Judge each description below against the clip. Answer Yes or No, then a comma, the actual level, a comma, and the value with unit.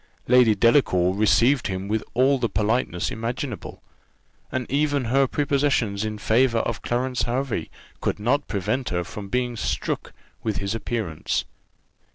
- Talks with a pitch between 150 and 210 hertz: No, low, 115 Hz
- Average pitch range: Yes, average, 3.7 semitones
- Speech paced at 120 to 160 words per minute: Yes, average, 140 wpm